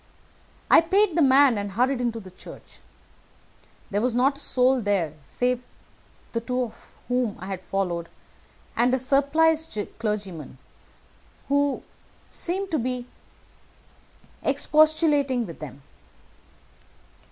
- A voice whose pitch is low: No, very high, 250 Hz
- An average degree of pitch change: No, wide, 5.7 semitones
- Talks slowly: Yes, slow, 115 wpm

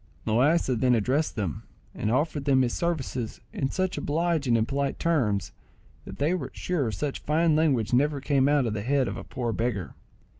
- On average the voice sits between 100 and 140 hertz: Yes, low, 135 Hz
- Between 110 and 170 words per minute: No, average, 185 wpm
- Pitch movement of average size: Yes, average, 4.4 semitones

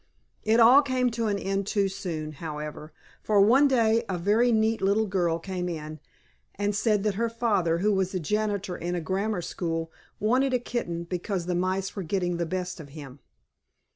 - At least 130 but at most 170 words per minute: No, average, 185 wpm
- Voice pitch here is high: Yes, high, 195 Hz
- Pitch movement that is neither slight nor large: Yes, average, 4.1 semitones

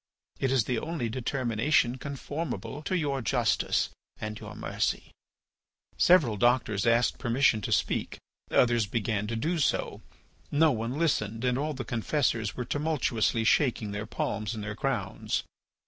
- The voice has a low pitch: Yes, low, 120 Hz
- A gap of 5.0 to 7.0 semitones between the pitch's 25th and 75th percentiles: No, average, 4.2 semitones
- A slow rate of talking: No, average, 145 wpm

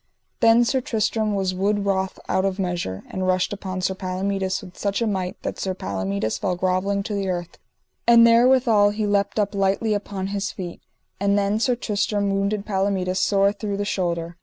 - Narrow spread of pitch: Yes, narrow, 1.8 semitones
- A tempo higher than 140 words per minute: Yes, average, 185 wpm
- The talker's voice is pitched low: No, high, 200 Hz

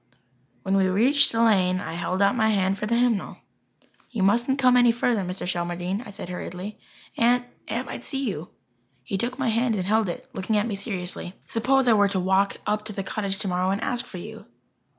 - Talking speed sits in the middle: No, fast, 210 wpm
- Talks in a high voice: Yes, high, 205 Hz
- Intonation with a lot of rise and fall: No, average, 3.7 semitones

